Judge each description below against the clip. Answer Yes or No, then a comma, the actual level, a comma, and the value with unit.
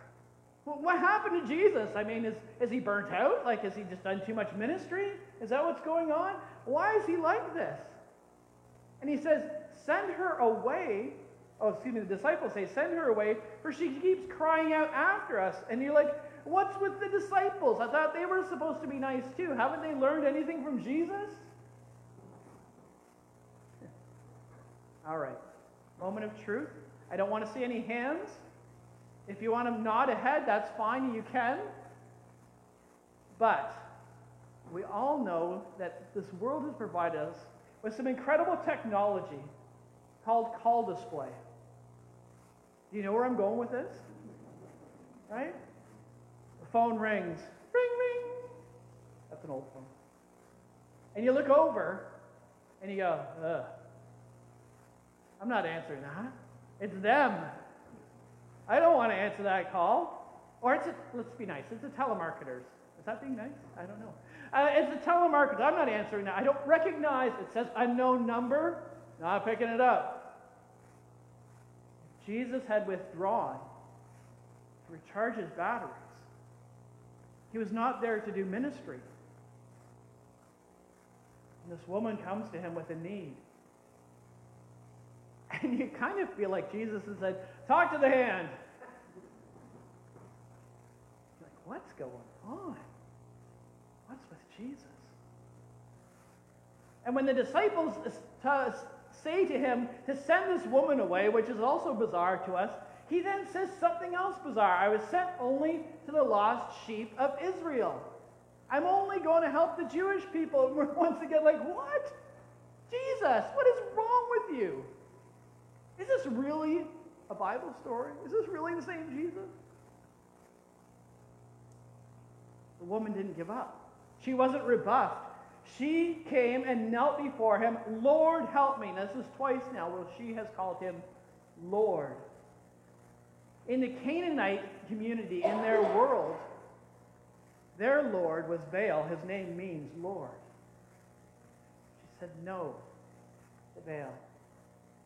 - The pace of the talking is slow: No, average, 145 wpm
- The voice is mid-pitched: No, high, 210 Hz